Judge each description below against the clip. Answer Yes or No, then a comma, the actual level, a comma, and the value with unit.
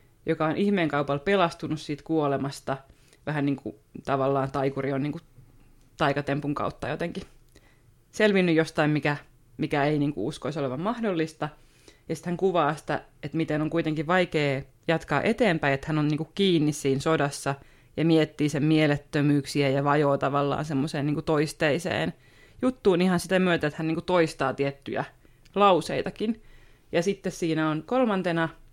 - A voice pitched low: No, medium, 150 Hz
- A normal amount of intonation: Yes, average, 3.0 semitones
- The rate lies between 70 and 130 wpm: No, fast, 155 wpm